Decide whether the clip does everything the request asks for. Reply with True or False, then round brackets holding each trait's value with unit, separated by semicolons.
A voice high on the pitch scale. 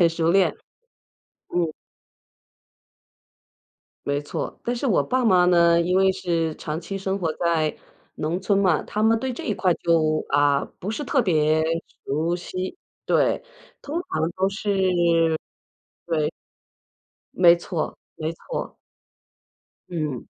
False (175 Hz)